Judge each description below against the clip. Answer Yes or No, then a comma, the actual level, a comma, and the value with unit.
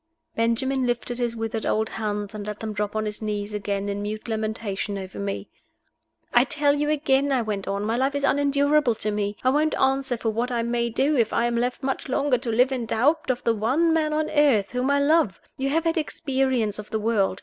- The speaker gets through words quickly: Yes, fast, 225 wpm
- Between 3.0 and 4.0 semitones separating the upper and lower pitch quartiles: No, average, 4.4 semitones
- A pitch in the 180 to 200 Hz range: No, high, 235 Hz